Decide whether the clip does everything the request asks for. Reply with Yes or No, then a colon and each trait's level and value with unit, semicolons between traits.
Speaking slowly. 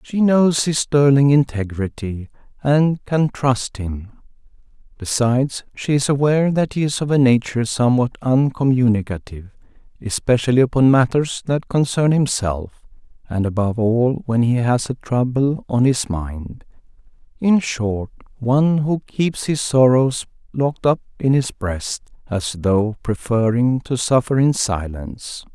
Yes: slow, 130 wpm